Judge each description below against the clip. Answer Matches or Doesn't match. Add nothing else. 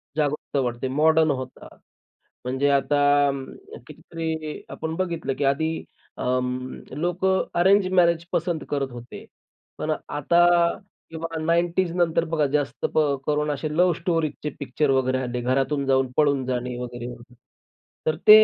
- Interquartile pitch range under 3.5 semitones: Doesn't match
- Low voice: Doesn't match